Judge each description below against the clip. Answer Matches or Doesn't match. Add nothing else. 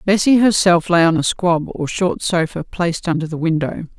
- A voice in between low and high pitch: Matches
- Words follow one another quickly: Doesn't match